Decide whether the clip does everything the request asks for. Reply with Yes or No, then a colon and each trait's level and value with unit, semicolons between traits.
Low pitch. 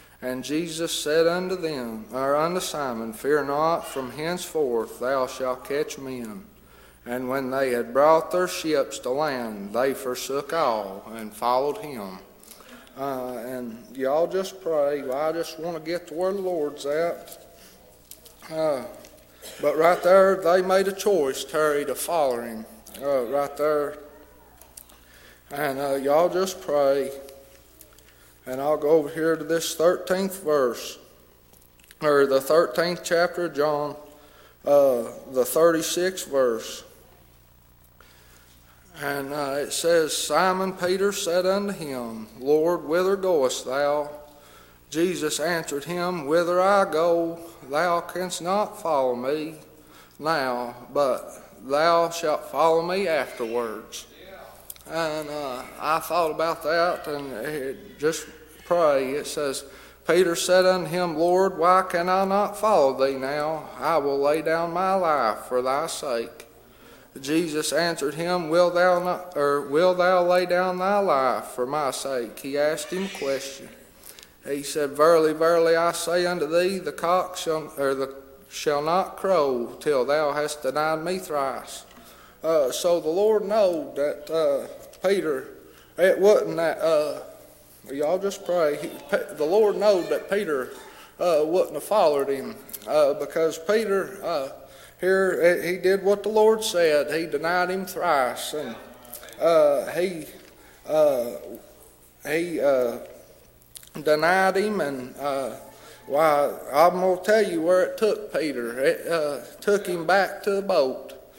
No: medium, 160 Hz